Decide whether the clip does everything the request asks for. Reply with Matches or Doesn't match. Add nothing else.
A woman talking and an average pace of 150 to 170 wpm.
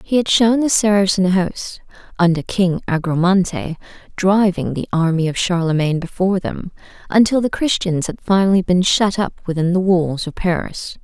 Matches